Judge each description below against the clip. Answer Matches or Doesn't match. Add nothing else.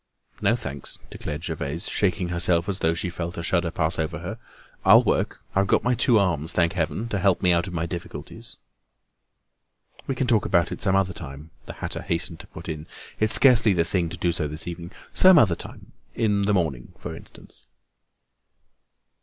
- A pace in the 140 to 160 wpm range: Doesn't match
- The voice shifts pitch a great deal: Doesn't match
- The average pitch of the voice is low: Matches